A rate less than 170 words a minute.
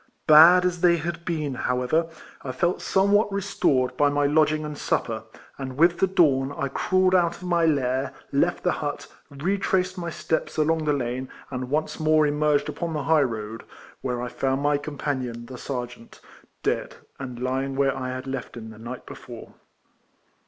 No: average, 180 wpm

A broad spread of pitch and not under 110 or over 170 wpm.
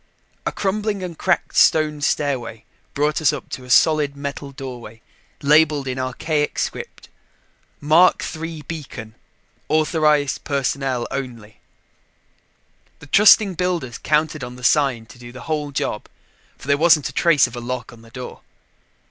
No: average, 3.7 semitones; average, 150 wpm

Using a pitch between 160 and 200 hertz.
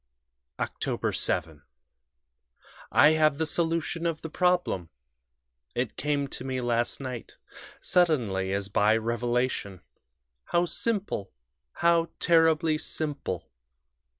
No: medium, 140 Hz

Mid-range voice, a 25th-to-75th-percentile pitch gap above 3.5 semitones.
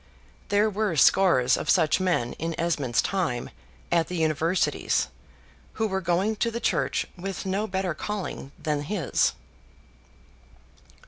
Yes: medium, 180 Hz; average, 3.9 semitones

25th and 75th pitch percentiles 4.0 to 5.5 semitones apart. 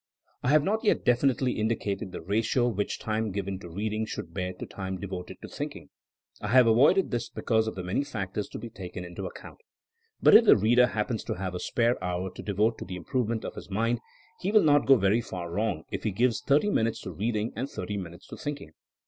Yes: average, 4.4 semitones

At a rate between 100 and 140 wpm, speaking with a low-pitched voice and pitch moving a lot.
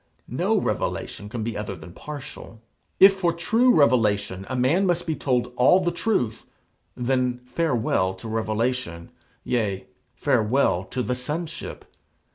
Yes: slow, 135 wpm; low, 125 Hz; wide, 6.7 semitones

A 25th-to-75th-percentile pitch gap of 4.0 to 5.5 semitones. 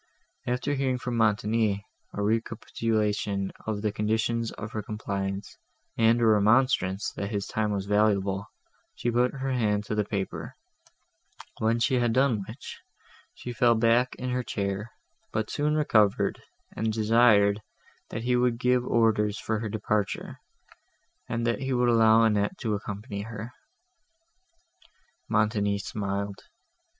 No: narrow, 2.5 semitones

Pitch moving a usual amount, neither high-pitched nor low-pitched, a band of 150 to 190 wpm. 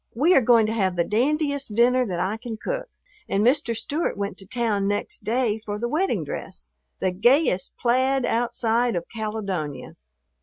No: average, 3.9 semitones; high, 230 Hz; average, 175 wpm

